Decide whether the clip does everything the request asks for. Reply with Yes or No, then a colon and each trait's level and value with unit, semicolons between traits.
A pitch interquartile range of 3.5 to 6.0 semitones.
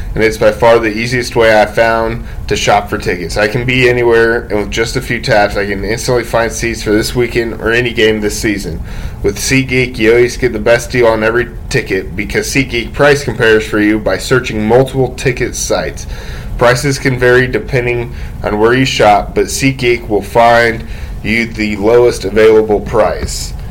No: narrow, 2.5 semitones